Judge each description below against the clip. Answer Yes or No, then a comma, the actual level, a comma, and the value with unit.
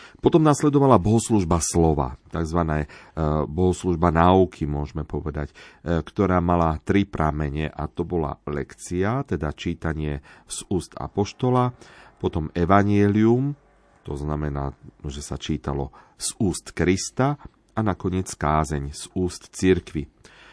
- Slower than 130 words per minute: Yes, slow, 110 wpm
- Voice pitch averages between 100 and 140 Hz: No, very low, 85 Hz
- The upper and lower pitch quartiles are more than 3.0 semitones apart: Yes, average, 4.7 semitones